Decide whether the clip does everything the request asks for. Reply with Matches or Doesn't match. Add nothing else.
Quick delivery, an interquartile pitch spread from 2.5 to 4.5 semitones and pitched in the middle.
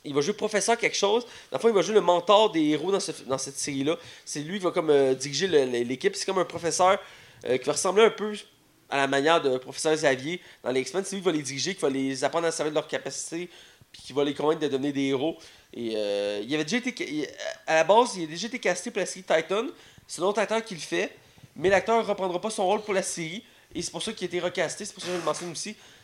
Doesn't match